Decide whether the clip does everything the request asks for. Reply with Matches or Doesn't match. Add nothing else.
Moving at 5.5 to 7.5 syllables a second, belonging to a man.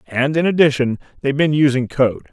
Matches